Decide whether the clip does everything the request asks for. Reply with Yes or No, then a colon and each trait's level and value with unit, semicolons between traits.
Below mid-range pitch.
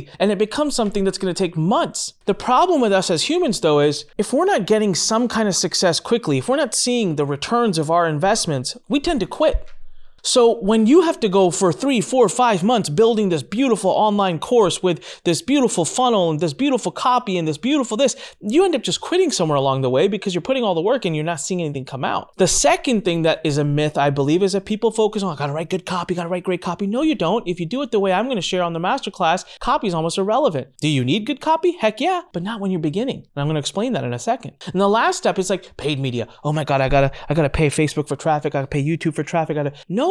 No: high, 190 Hz